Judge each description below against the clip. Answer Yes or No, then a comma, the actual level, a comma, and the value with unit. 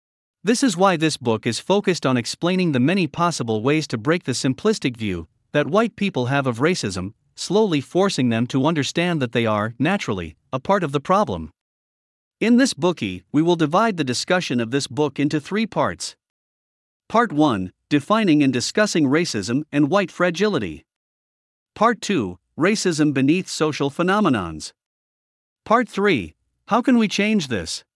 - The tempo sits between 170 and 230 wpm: No, average, 160 wpm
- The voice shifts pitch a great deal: Yes, wide, 7.6 semitones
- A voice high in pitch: No, medium, 150 Hz